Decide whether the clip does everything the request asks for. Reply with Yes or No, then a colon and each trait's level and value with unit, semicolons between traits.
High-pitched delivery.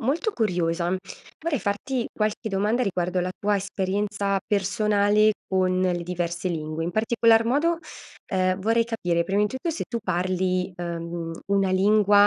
Yes: high, 195 Hz